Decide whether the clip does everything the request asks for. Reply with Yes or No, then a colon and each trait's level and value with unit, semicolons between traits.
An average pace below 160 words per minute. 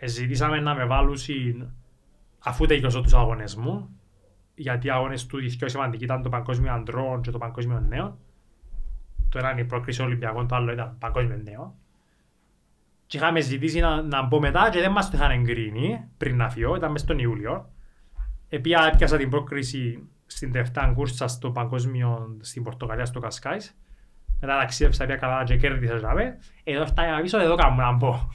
No: average, 165 wpm